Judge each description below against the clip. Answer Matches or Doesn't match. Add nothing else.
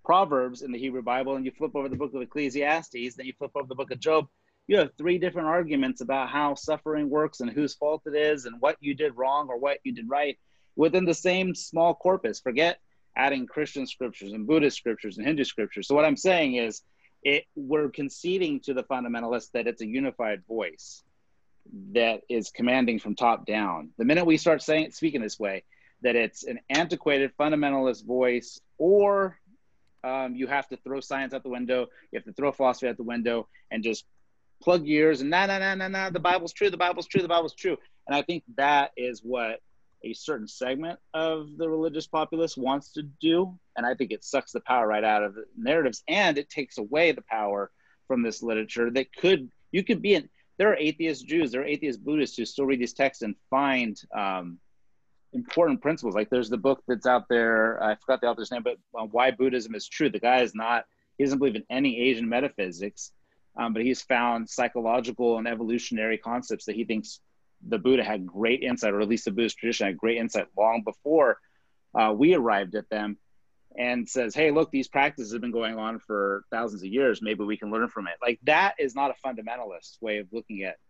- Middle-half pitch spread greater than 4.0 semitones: Matches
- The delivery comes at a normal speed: Doesn't match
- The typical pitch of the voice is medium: Doesn't match